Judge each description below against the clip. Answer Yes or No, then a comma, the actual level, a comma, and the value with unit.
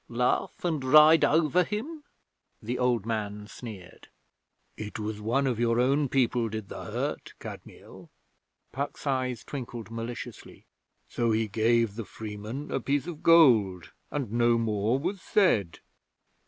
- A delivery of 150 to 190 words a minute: No, average, 140 wpm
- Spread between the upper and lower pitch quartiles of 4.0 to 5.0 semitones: Yes, average, 4.4 semitones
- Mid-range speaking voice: No, low, 120 Hz